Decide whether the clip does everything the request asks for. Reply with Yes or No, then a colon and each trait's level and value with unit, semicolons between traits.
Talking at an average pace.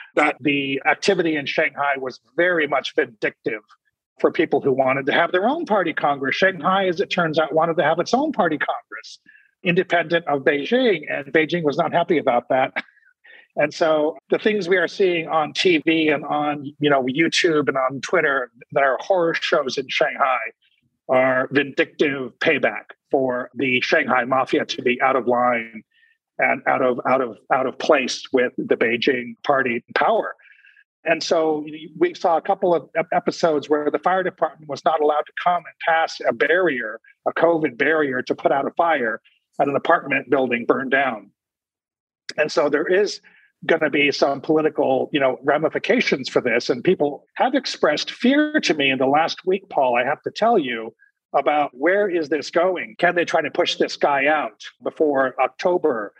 Yes: average, 185 wpm